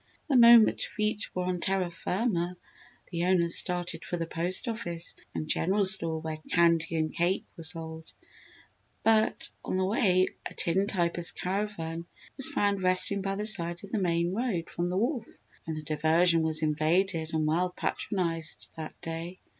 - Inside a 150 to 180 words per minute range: Yes, average, 165 wpm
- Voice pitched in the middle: Yes, medium, 175 Hz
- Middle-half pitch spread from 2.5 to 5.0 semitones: Yes, average, 2.9 semitones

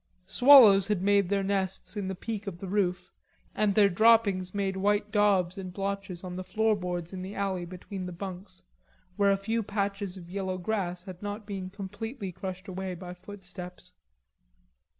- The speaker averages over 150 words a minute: Yes, average, 175 wpm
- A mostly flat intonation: Yes, narrow, 1.9 semitones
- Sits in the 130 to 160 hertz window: No, high, 195 Hz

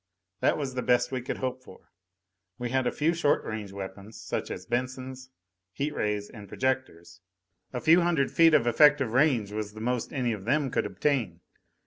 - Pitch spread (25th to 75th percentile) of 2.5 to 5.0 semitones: Yes, average, 4.2 semitones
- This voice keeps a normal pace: Yes, average, 185 wpm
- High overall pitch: No, low, 125 Hz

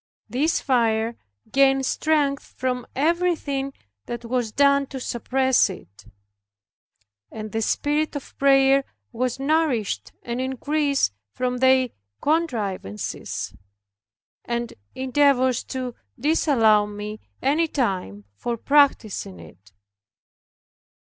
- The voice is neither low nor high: No, very high, 260 Hz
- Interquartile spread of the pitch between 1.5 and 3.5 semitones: No, average, 3.9 semitones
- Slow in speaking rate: Yes, slow, 95 wpm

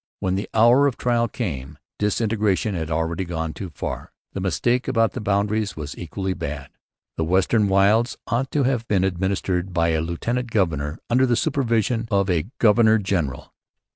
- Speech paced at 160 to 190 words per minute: Yes, average, 170 wpm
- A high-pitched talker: No, low, 100 Hz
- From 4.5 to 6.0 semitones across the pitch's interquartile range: Yes, average, 5.2 semitones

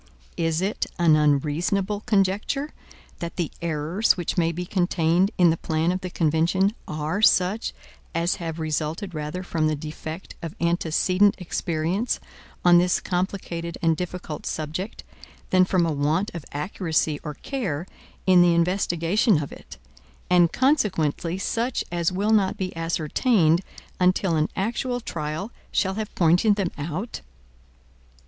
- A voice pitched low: No, medium, 175 Hz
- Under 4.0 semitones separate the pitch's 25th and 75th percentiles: Yes, average, 3.2 semitones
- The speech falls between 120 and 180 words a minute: Yes, average, 140 wpm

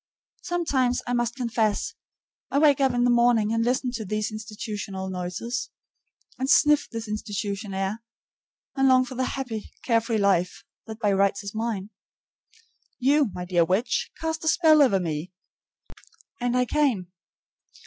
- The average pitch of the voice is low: No, high, 230 Hz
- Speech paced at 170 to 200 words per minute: No, average, 150 wpm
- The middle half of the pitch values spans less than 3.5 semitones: No, average, 4.1 semitones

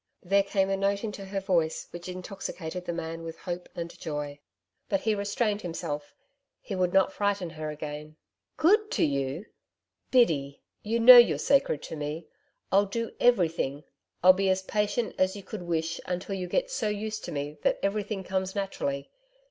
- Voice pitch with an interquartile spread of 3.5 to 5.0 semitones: Yes, average, 3.9 semitones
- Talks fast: No, average, 175 wpm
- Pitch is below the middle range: No, medium, 185 Hz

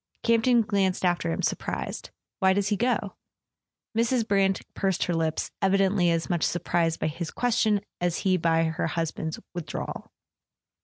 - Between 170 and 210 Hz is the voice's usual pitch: Yes, high, 190 Hz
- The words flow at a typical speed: Yes, average, 160 wpm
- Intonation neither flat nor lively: Yes, average, 3.8 semitones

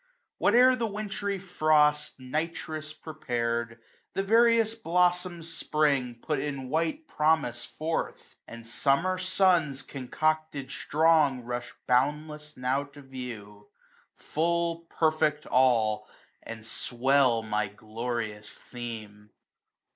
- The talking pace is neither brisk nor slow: No, slow, 110 wpm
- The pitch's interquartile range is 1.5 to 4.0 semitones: No, wide, 5.4 semitones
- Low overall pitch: No, medium, 150 Hz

